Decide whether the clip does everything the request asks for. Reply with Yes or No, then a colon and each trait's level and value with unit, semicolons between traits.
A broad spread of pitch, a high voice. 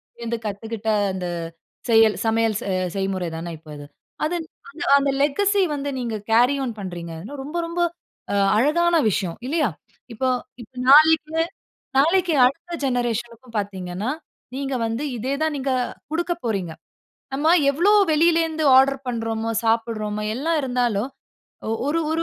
Yes: wide, 6.0 semitones; high, 245 Hz